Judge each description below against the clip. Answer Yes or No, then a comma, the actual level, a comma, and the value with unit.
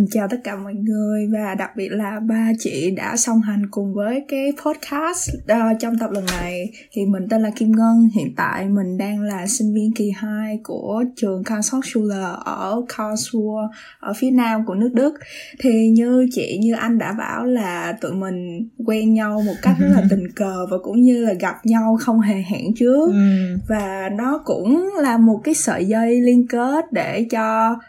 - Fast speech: No, average, 190 wpm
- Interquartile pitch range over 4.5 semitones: No, average, 2.7 semitones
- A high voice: Yes, high, 220 Hz